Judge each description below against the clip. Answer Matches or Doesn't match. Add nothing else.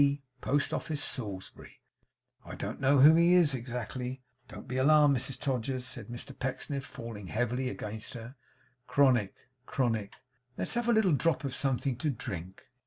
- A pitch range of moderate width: Matches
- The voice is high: Doesn't match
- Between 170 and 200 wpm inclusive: Doesn't match